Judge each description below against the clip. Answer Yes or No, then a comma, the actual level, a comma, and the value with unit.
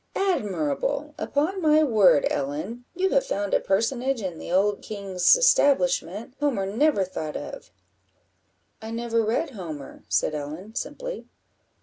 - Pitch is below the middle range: No, high, 220 Hz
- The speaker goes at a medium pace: No, slow, 130 wpm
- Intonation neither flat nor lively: No, wide, 7.4 semitones